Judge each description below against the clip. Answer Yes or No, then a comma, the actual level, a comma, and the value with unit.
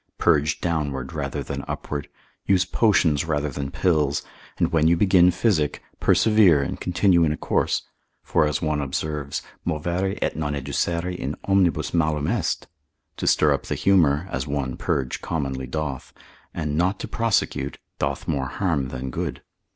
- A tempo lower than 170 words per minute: Yes, average, 160 wpm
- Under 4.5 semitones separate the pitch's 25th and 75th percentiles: Yes, average, 3.8 semitones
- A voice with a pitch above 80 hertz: No, very low, 75 Hz